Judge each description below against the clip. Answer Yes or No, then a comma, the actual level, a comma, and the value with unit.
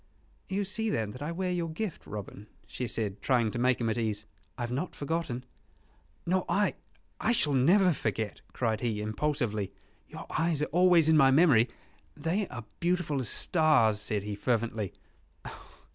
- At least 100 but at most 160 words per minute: No, average, 175 wpm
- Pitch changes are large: Yes, wide, 7.4 semitones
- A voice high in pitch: No, low, 130 Hz